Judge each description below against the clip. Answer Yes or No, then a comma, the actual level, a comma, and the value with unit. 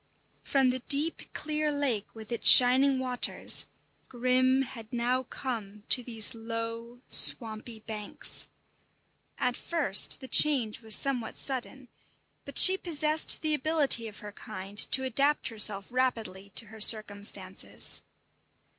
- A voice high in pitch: Yes, high, 245 Hz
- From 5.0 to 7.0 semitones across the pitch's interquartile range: No, average, 3.6 semitones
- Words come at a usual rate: No, slow, 130 wpm